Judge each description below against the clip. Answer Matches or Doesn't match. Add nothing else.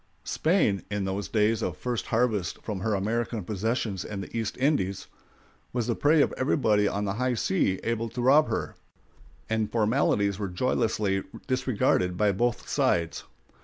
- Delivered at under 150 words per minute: Doesn't match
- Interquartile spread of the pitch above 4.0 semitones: Doesn't match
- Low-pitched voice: Matches